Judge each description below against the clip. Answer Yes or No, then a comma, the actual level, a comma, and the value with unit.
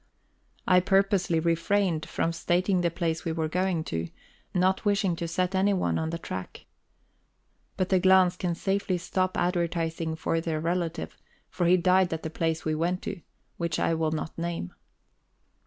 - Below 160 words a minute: No, average, 165 wpm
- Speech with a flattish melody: Yes, narrow, 2.2 semitones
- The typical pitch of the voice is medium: Yes, medium, 175 Hz